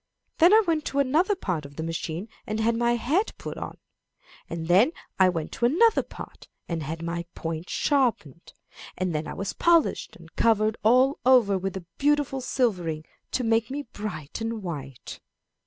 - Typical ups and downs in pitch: No, wide, 7.9 semitones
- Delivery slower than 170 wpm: No, average, 175 wpm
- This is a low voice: No, high, 215 Hz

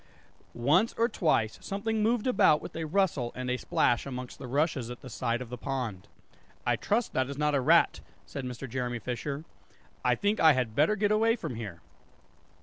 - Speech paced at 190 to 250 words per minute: Yes, average, 195 wpm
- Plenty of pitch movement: Yes, wide, 7.7 semitones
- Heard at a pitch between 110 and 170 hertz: Yes, medium, 140 Hz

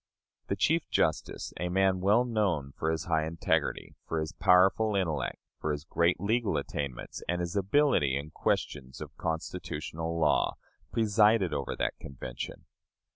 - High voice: No, very low, 85 Hz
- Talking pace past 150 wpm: No, average, 145 wpm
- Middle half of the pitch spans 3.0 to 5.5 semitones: Yes, average, 4.6 semitones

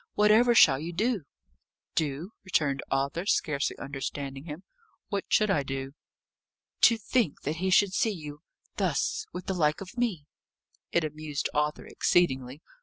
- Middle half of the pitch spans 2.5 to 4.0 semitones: No, wide, 5.6 semitones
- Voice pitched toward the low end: No, medium, 160 Hz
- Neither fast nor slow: Yes, average, 145 wpm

